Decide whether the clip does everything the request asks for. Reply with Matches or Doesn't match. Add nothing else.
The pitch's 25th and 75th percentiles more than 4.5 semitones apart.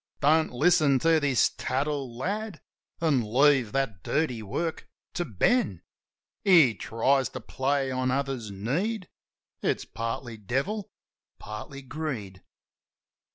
Matches